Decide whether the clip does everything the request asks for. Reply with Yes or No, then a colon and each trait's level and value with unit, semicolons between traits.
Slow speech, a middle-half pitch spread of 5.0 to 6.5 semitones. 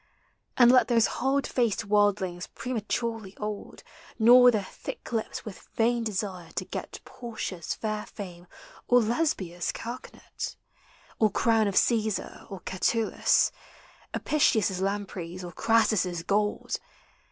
No: slow, 120 wpm; average, 3.5 semitones